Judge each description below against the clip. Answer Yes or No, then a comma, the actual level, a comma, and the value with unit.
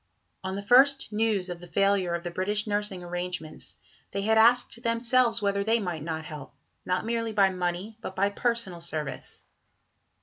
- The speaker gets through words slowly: No, average, 170 wpm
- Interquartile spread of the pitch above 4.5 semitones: No, average, 4.1 semitones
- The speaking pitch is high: Yes, high, 200 Hz